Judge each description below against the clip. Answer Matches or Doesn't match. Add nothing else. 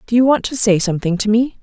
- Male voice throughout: Doesn't match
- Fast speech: Matches